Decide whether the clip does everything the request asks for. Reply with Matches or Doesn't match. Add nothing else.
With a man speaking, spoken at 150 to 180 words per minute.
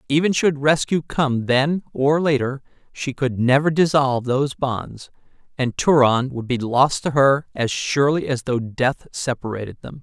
Matches